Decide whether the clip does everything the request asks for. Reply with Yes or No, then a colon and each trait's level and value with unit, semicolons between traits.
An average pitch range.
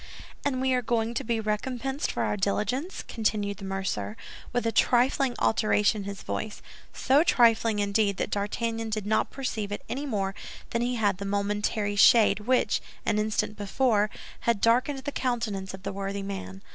Yes: average, 3.2 semitones